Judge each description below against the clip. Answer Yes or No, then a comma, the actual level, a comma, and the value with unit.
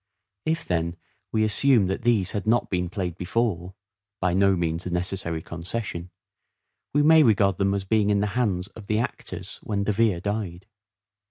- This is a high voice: No, low, 100 Hz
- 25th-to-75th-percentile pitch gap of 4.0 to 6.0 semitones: No, average, 3.6 semitones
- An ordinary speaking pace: Yes, average, 175 wpm